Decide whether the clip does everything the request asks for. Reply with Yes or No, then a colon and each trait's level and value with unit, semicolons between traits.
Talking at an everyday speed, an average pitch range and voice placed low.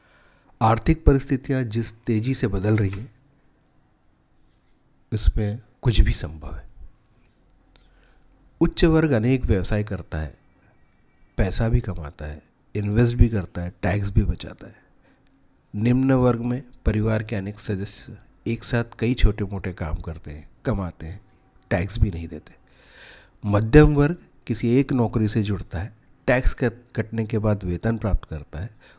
Yes: average, 145 wpm; average, 4.4 semitones; low, 110 Hz